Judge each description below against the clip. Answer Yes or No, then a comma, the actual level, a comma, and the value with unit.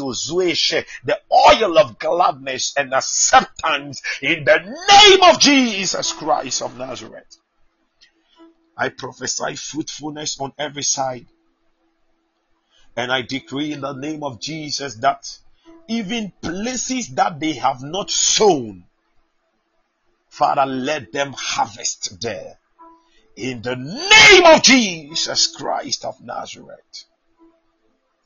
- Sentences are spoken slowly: Yes, slow, 105 wpm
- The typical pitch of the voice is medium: Yes, medium, 165 Hz